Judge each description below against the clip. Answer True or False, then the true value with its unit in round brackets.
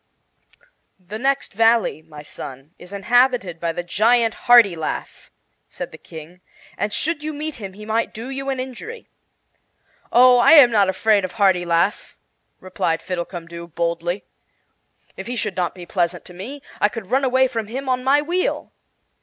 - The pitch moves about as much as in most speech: False (6.3 semitones)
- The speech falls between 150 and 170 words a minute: True (160 wpm)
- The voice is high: True (210 Hz)